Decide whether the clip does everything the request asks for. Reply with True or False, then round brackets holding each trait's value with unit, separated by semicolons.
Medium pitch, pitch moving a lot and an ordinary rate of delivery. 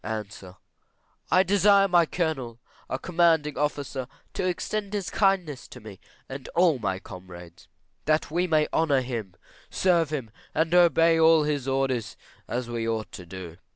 True (150 Hz; 6.7 semitones; 155 wpm)